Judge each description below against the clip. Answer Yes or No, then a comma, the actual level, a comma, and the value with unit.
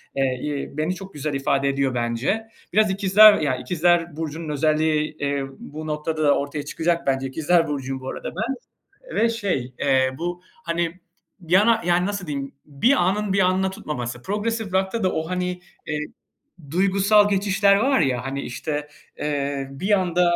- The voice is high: No, medium, 165 Hz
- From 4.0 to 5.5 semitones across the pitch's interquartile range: Yes, average, 5.2 semitones